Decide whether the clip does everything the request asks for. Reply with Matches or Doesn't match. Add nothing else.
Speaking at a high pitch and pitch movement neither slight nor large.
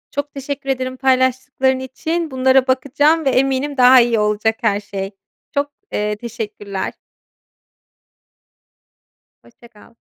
Matches